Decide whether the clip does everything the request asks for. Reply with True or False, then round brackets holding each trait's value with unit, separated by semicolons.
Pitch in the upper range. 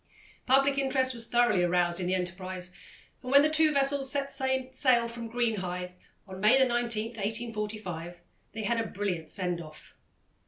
True (225 Hz)